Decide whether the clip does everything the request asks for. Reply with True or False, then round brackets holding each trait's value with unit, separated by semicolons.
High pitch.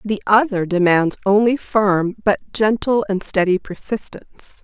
True (205 Hz)